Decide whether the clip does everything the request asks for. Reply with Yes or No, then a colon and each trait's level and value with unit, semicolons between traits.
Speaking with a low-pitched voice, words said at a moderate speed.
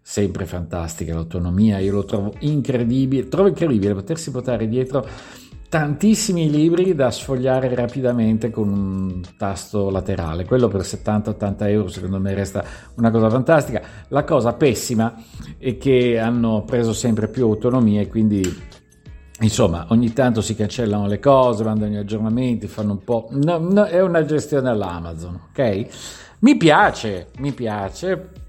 Yes: low, 110 Hz; average, 135 wpm